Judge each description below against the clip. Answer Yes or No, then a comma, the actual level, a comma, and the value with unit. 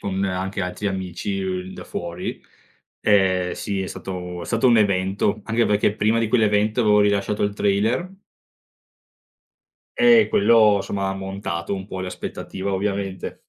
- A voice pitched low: Yes, low, 100 Hz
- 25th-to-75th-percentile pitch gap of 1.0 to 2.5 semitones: Yes, narrow, 1.9 semitones